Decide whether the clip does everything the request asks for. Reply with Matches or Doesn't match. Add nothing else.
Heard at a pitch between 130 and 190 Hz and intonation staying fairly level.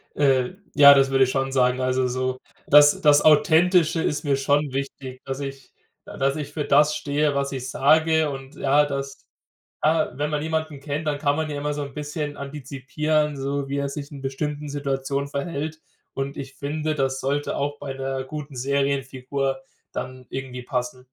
Matches